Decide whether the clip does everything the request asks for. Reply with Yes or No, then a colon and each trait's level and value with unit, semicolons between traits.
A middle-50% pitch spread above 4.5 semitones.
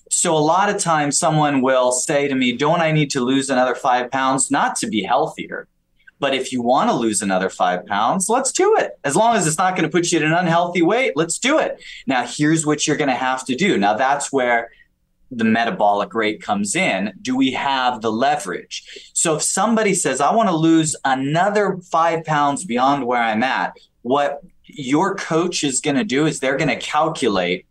Yes: average, 5.2 semitones